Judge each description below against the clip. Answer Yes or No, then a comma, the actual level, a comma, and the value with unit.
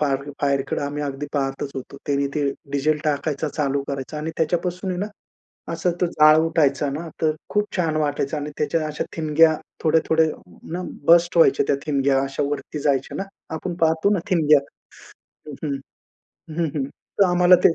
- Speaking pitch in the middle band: Yes, medium, 150 Hz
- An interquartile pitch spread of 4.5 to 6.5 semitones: No, narrow, 2.6 semitones